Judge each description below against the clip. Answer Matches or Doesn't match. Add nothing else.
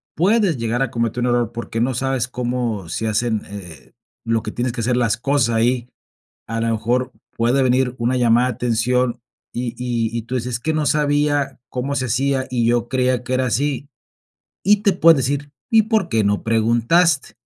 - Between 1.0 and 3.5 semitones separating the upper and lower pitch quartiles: Matches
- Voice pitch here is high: Doesn't match